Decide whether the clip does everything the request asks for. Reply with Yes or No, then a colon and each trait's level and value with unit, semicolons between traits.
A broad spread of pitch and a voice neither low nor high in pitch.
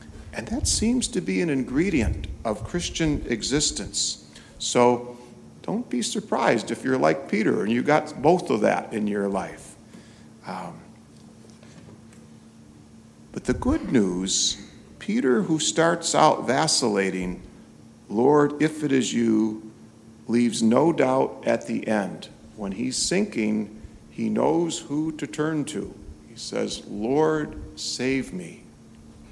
No: wide, 7.9 semitones; low, 120 Hz